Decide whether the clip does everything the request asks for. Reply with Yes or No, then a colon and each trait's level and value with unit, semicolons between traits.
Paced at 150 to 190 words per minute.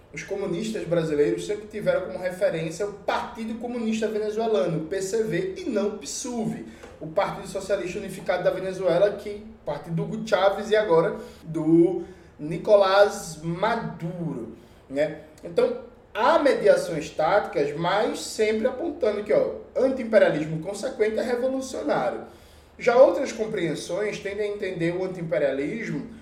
No: average, 125 wpm